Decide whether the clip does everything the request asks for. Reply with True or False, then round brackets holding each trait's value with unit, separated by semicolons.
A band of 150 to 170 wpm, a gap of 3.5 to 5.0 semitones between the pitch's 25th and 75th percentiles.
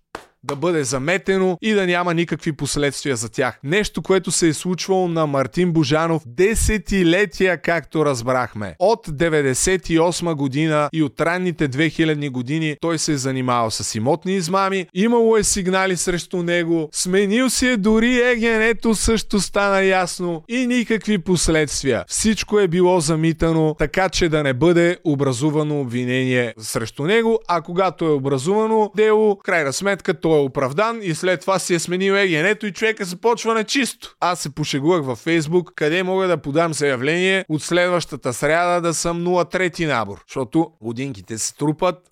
True (155 wpm; 4.2 semitones)